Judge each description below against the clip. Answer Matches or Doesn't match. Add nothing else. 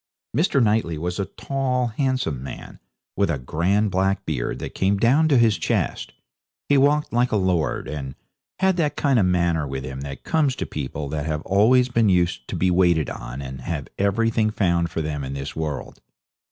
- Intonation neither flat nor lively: Doesn't match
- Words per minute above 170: Matches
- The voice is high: Doesn't match